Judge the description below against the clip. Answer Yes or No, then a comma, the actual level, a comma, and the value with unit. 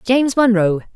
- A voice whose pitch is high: Yes, high, 220 Hz